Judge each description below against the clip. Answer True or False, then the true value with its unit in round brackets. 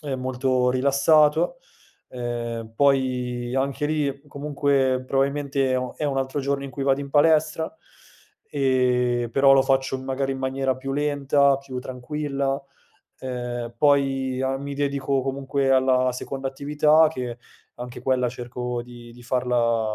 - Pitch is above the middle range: False (135 Hz)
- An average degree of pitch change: False (1.9 semitones)